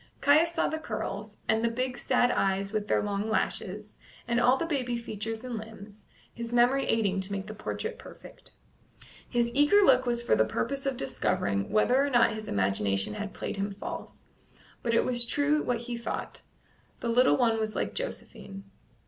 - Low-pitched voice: No, high, 230 Hz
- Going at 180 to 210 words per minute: Yes, average, 190 wpm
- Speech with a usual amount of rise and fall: Yes, average, 3.6 semitones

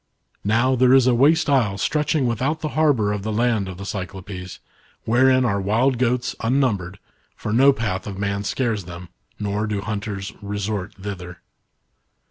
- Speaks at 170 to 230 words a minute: No, average, 160 wpm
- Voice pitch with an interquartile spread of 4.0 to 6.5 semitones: Yes, average, 4.4 semitones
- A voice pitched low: Yes, low, 105 Hz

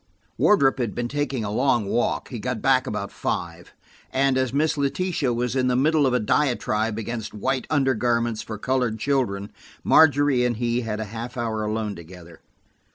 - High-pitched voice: No, low, 120 Hz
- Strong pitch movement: No, average, 3.5 semitones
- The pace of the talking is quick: No, average, 175 wpm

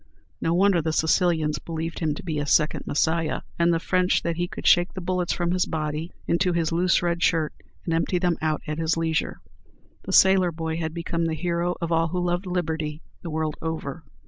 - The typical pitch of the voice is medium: Yes, medium, 165 Hz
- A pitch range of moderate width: No, narrow, 1.7 semitones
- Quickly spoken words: Yes, fast, 210 wpm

